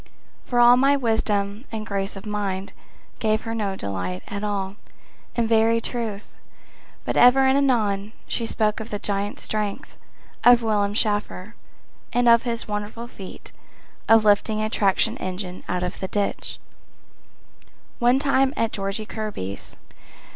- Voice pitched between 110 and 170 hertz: No, high, 215 Hz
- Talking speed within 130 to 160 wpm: Yes, average, 145 wpm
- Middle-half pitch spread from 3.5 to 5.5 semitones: No, narrow, 2.6 semitones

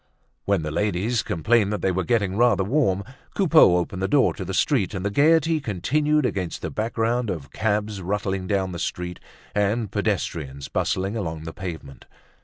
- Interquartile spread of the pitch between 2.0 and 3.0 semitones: No, average, 4.3 semitones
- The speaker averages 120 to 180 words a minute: Yes, average, 175 wpm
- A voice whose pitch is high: No, low, 100 Hz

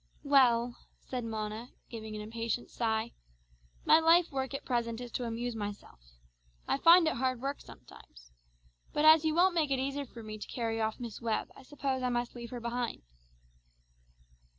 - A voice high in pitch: Yes, high, 240 Hz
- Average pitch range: Yes, average, 3.3 semitones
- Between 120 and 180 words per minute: Yes, average, 175 wpm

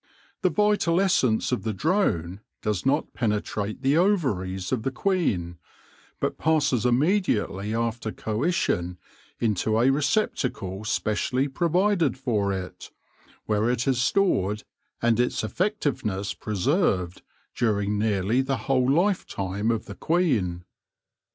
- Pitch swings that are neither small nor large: No, wide, 6.7 semitones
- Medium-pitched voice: No, low, 120 Hz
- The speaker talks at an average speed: No, slow, 120 wpm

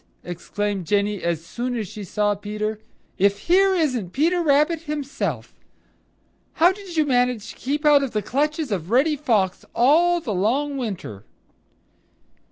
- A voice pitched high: Yes, high, 245 Hz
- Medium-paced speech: Yes, average, 150 wpm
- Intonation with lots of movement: Yes, wide, 6.7 semitones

